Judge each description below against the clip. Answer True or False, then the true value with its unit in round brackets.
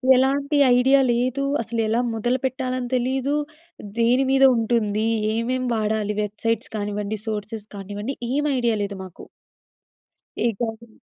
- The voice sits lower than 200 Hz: False (230 Hz)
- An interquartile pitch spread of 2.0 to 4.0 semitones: True (3.3 semitones)